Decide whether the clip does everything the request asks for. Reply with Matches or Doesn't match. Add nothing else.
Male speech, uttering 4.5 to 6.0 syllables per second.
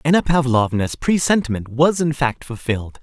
Matches